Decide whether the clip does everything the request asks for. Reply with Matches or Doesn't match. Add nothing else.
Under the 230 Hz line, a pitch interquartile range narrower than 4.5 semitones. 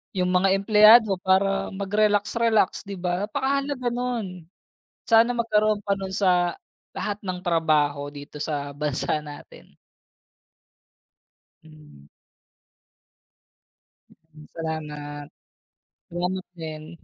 Doesn't match